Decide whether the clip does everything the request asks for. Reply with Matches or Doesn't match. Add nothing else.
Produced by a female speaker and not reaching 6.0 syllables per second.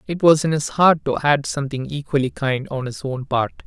Doesn't match